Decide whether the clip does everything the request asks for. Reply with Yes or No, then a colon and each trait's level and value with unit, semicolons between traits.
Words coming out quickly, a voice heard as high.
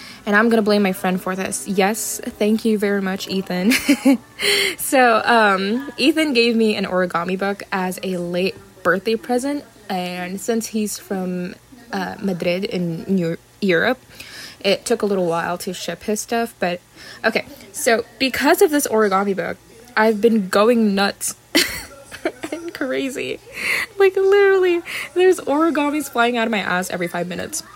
No: average, 155 wpm; high, 215 Hz